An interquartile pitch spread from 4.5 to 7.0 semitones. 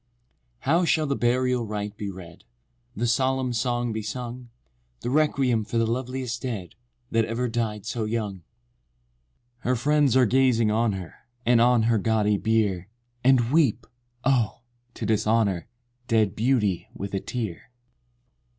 No: average, 2.9 semitones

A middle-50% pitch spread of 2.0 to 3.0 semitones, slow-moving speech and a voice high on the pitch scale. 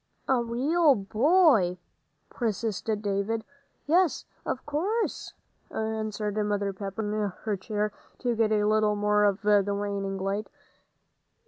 Yes: narrow, 2.5 semitones; slow, 120 wpm; high, 215 Hz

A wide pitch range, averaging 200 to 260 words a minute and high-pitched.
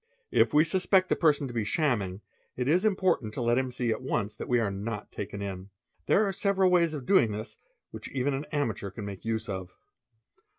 No: wide, 7.1 semitones; fast, 205 wpm; low, 120 Hz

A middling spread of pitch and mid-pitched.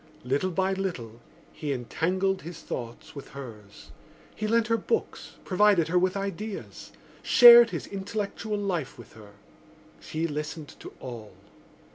No: wide, 6.7 semitones; medium, 180 Hz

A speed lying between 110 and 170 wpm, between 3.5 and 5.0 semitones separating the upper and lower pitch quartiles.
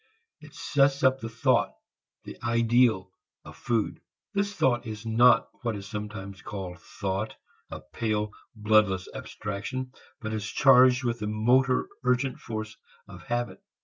No: average, 140 wpm; average, 3.1 semitones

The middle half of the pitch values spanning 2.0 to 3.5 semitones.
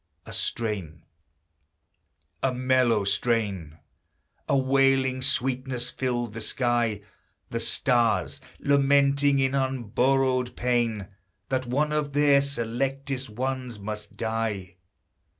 Yes: average, 3.0 semitones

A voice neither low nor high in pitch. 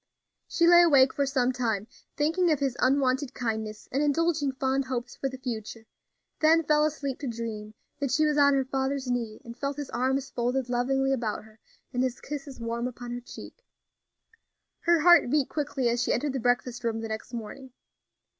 No: very high, 260 Hz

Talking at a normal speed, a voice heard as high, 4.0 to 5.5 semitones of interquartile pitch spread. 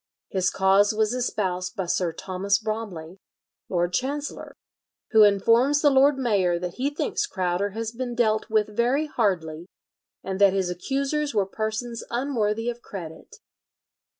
Yes: average, 145 wpm; high, 215 Hz; average, 4.5 semitones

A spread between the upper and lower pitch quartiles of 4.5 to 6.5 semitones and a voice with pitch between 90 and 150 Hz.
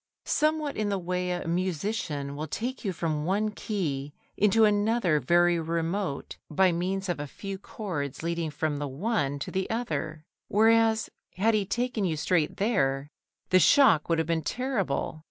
No: wide, 5.4 semitones; medium, 180 Hz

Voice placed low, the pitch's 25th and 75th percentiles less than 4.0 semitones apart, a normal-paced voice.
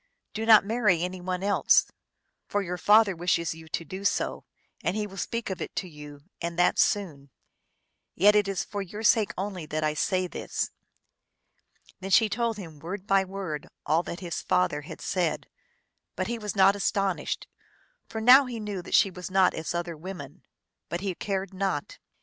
No: high, 190 Hz; average, 3.2 semitones; average, 185 wpm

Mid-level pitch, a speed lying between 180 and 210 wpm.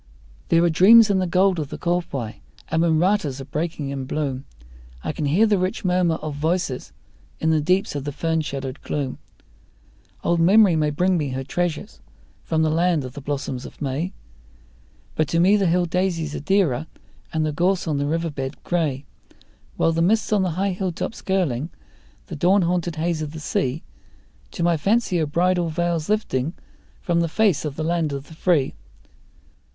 Yes: medium, 165 Hz; average, 190 wpm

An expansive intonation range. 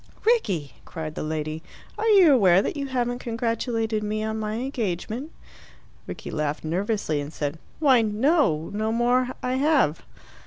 Yes: wide, 7.4 semitones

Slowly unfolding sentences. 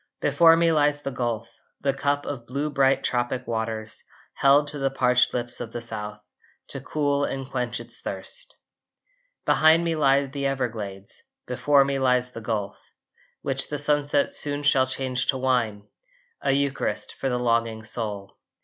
No: average, 160 wpm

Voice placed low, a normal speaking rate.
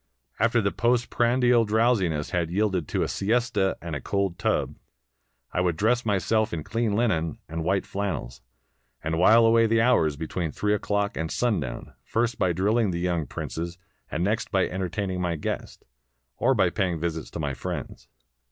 Yes: very low, 95 Hz; average, 175 wpm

